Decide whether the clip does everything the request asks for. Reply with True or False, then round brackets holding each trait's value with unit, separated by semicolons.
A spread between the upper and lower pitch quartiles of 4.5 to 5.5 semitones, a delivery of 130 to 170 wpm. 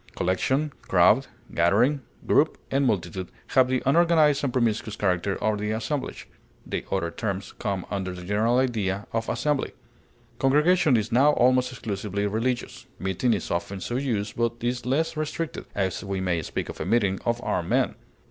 True (5.2 semitones; 165 wpm)